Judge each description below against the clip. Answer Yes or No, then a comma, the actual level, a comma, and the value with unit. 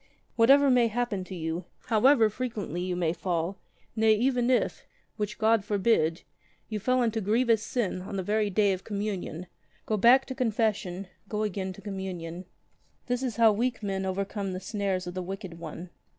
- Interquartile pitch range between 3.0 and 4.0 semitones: Yes, average, 3.7 semitones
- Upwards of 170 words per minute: Yes, average, 180 wpm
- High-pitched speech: Yes, high, 205 Hz